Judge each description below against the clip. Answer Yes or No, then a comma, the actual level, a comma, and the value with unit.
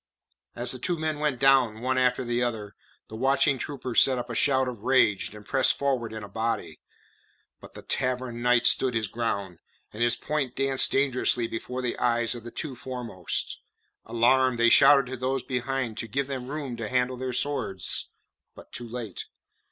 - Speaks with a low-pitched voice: Yes, low, 125 Hz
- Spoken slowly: No, average, 185 wpm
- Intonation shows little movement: Yes, narrow, 2.2 semitones